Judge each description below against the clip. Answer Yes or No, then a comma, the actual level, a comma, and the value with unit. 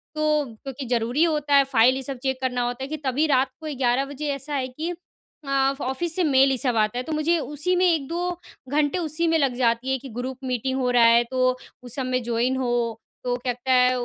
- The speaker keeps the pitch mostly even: No, average, 3.2 semitones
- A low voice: No, very high, 265 Hz